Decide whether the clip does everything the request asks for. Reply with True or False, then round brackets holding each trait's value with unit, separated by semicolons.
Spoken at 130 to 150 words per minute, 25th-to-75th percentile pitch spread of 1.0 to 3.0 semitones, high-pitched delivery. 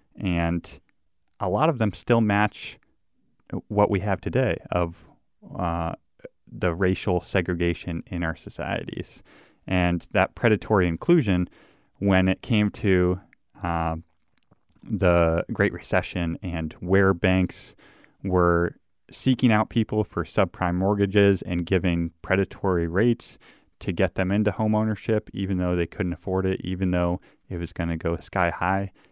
False (135 wpm; 2.6 semitones; 95 Hz)